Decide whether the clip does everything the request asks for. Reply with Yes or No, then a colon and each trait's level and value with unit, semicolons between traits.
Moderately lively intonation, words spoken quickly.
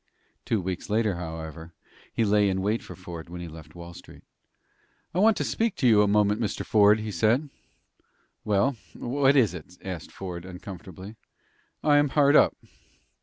No: average, 4.6 semitones; average, 170 wpm